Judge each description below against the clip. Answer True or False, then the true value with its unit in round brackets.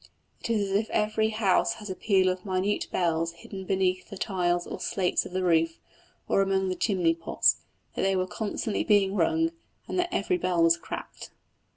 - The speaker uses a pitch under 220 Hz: True (190 Hz)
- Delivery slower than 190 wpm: False (195 wpm)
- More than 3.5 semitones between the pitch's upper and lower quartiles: False (2.6 semitones)